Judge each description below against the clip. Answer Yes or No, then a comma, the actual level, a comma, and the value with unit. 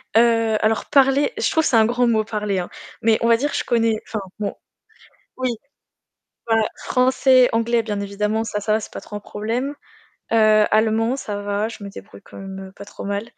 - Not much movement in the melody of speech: Yes, narrow, 2.2 semitones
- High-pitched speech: Yes, high, 220 Hz